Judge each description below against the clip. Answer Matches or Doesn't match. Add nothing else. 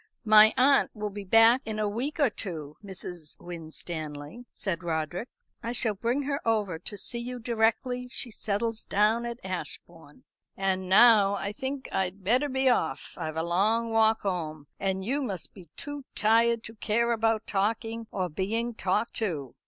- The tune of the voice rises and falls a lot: Doesn't match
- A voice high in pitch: Matches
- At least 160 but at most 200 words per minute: Matches